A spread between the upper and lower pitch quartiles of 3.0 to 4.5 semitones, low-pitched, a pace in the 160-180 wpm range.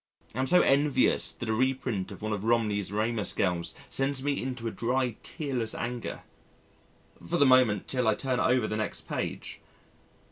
Yes: average, 3.5 semitones; low, 120 Hz; average, 175 wpm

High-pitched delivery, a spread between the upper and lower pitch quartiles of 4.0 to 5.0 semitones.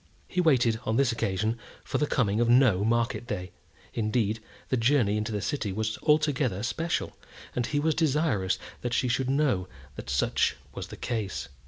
No: low, 120 Hz; average, 4.3 semitones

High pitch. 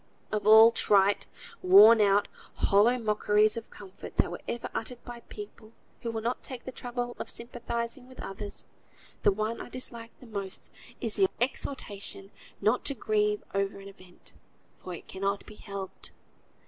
Yes: high, 215 Hz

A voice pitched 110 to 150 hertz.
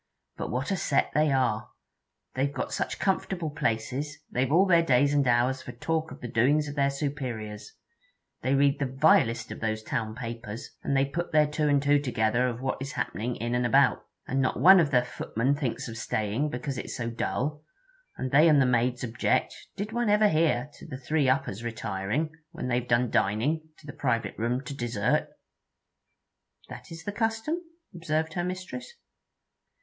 Yes: low, 135 Hz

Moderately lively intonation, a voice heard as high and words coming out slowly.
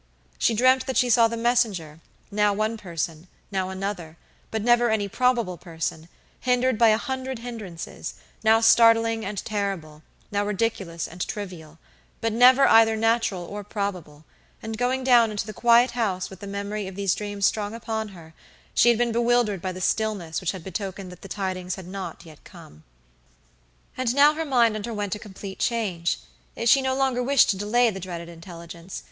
No: average, 4.0 semitones; high, 210 Hz; average, 175 wpm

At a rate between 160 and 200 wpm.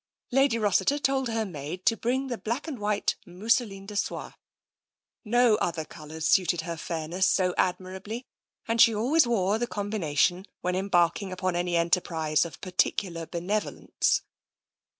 No: average, 150 wpm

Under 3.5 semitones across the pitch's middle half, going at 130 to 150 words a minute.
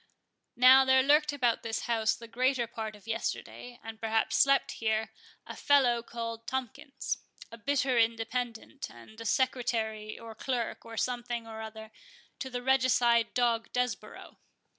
Yes: narrow, 2.4 semitones; average, 140 wpm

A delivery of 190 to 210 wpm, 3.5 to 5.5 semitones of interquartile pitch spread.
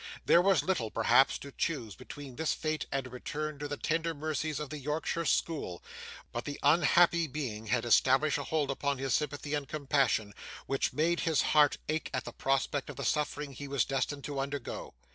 No: average, 195 wpm; narrow, 2.4 semitones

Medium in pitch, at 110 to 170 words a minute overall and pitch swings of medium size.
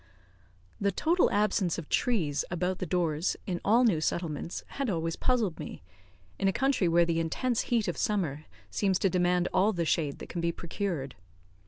No: medium, 180 Hz; average, 180 wpm; average, 3.8 semitones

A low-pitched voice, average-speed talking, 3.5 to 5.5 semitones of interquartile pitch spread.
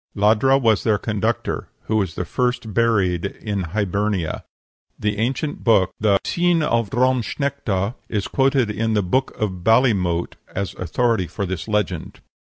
Yes: low, 105 Hz; average, 150 wpm; average, 3.8 semitones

